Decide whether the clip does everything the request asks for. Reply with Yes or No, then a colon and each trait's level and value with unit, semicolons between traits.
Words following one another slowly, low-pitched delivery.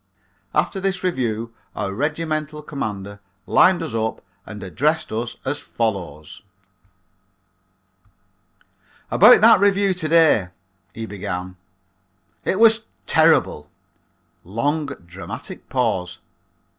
Yes: slow, 95 wpm; low, 125 Hz